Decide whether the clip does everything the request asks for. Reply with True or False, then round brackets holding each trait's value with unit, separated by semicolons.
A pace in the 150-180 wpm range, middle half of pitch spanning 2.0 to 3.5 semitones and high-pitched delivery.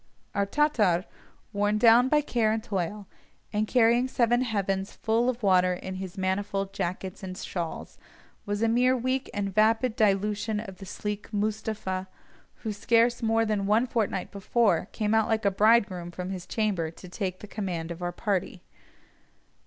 True (165 wpm; 3.0 semitones; 210 Hz)